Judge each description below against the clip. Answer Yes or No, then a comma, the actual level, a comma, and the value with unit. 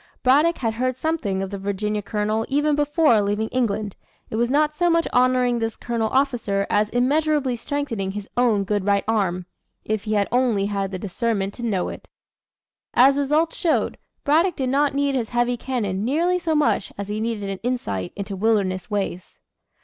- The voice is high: Yes, high, 230 Hz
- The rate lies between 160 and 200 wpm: Yes, average, 180 wpm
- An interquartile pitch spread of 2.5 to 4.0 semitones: No, average, 5.3 semitones